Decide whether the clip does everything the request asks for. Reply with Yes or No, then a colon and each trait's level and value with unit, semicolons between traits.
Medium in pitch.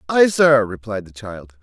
No: low, 120 Hz